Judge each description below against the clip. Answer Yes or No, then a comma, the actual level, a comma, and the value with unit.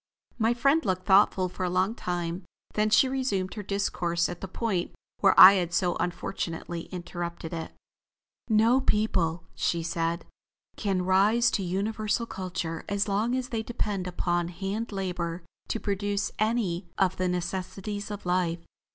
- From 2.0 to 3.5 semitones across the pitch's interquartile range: Yes, average, 3.2 semitones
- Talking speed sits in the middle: Yes, average, 150 wpm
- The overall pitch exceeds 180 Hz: Yes, high, 190 Hz